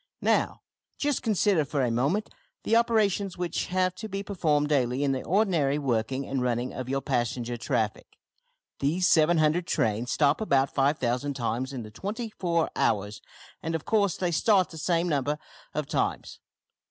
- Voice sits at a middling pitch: Yes, medium, 150 Hz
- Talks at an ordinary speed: Yes, average, 165 wpm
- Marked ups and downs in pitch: Yes, wide, 6.2 semitones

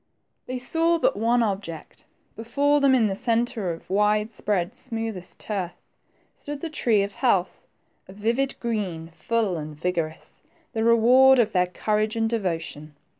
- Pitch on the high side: Yes, high, 215 Hz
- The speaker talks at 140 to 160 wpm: Yes, average, 155 wpm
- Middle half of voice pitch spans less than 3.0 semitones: No, average, 4.7 semitones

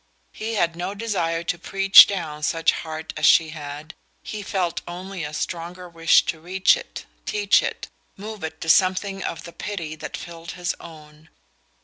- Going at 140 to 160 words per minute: No, average, 170 wpm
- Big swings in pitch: No, average, 3.3 semitones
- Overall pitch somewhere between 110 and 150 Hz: No, medium, 170 Hz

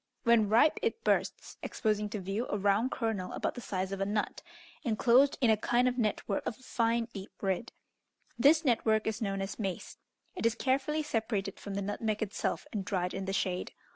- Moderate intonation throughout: Yes, average, 3.4 semitones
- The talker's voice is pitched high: Yes, high, 220 Hz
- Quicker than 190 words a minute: Yes, average, 200 wpm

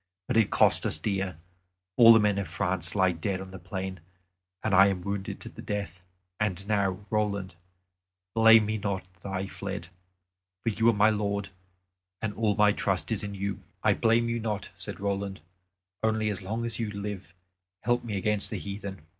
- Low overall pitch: Yes, low, 100 Hz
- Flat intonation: Yes, narrow, 2.1 semitones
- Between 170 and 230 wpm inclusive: Yes, average, 190 wpm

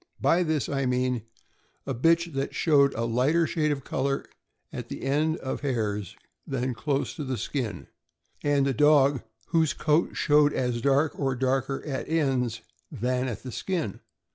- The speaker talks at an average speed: Yes, average, 165 wpm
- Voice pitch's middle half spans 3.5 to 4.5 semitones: No, average, 2.9 semitones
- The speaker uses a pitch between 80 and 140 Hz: Yes, low, 135 Hz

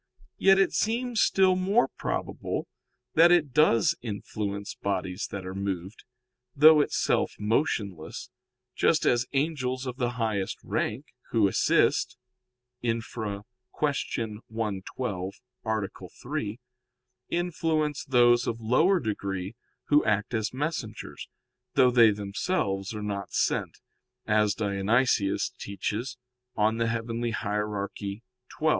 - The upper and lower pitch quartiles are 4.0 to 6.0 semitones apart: Yes, average, 4.9 semitones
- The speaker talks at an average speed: No, slow, 110 wpm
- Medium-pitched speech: No, low, 115 Hz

